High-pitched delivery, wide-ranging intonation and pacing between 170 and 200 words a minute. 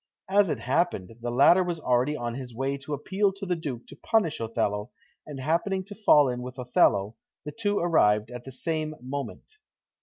No: medium, 140 Hz; wide, 6.1 semitones; average, 190 wpm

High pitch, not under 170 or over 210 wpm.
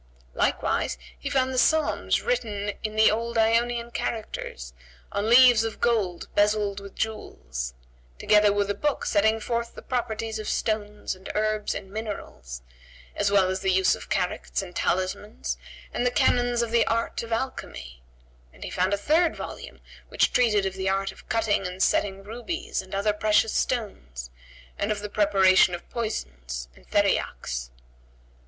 No: high, 210 Hz; average, 160 wpm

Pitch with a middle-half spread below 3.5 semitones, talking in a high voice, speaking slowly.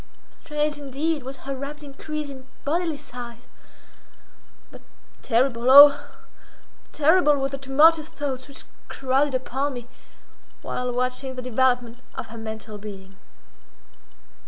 Yes: average, 2.8 semitones; very high, 270 Hz; slow, 115 wpm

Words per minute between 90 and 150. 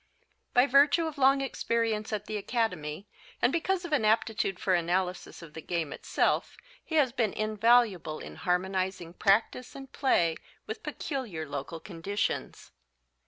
Yes: average, 145 wpm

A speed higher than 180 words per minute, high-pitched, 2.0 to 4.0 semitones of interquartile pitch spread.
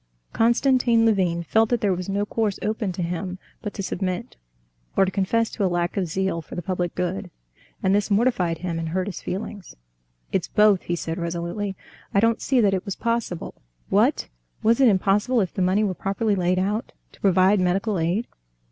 Yes: average, 195 wpm; high, 195 Hz; average, 3.1 semitones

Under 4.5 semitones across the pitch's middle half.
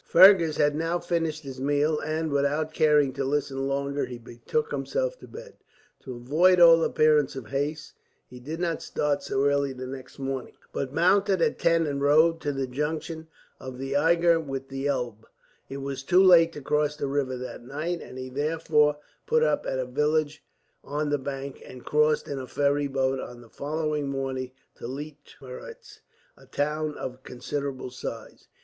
Yes: average, 2.8 semitones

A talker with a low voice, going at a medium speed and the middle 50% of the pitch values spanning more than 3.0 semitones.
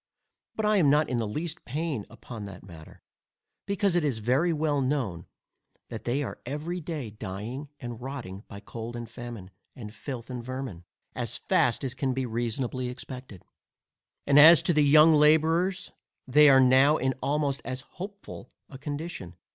Yes: low, 130 Hz; average, 170 wpm; average, 4.3 semitones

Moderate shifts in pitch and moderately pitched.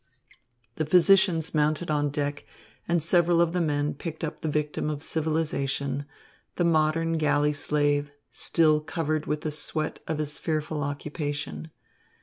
No: narrow, 1.8 semitones; medium, 155 Hz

